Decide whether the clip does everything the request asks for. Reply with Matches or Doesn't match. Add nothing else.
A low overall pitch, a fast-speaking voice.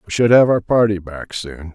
Matches